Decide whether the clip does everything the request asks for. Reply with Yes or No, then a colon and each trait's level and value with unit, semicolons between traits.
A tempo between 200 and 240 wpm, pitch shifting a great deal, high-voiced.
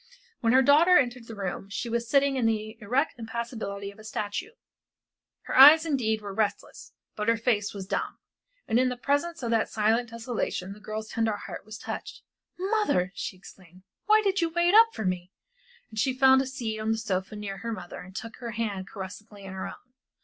No: fast, 205 wpm; average, 4.3 semitones; high, 225 Hz